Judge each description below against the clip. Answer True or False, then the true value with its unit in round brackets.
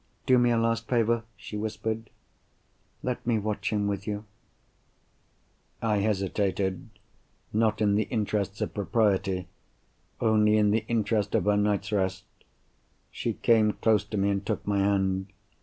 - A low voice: True (105 Hz)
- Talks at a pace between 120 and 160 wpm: True (140 wpm)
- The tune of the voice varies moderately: False (1.7 semitones)